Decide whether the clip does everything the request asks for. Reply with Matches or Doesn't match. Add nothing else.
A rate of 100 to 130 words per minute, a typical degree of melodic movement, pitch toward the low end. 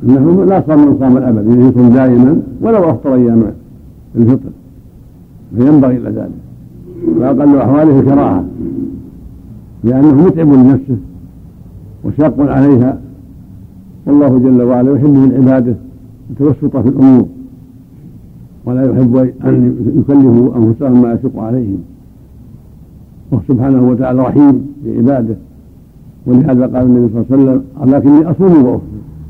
Matches